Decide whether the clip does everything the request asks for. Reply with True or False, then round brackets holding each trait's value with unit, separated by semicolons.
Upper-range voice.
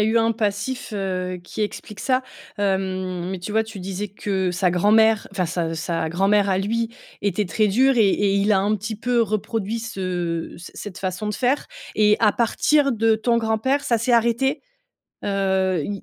True (205 Hz)